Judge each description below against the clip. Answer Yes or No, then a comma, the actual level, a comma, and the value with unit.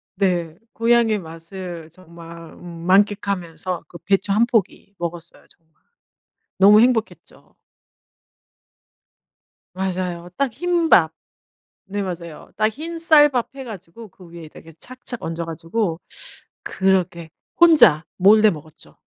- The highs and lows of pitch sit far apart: No, average, 4.9 semitones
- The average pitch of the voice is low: No, high, 190 Hz